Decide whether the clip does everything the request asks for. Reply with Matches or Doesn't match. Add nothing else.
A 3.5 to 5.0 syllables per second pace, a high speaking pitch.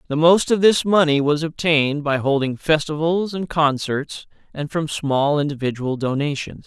Doesn't match